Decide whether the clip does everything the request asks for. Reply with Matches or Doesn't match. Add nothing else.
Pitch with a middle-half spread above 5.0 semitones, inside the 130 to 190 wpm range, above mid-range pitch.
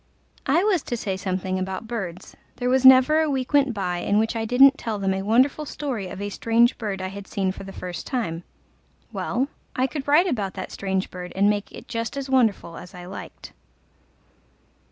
Doesn't match